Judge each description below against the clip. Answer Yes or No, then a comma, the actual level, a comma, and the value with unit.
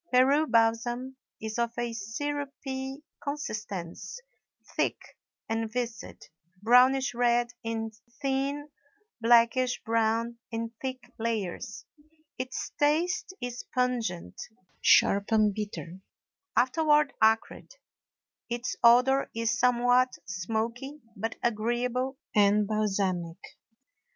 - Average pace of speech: No, slow, 90 wpm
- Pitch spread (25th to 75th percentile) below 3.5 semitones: Yes, average, 2.7 semitones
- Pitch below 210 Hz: No, high, 240 Hz